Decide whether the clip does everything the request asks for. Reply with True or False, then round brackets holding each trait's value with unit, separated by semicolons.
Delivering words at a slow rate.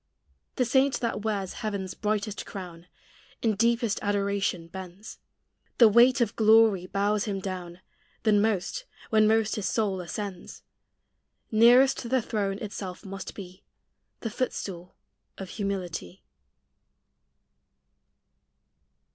True (110 wpm)